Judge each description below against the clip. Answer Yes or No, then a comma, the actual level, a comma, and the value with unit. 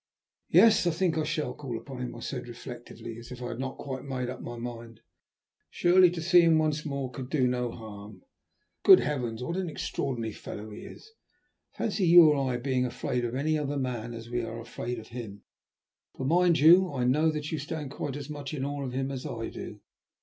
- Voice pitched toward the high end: No, low, 130 Hz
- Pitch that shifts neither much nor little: Yes, average, 4.3 semitones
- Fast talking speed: Yes, fast, 215 wpm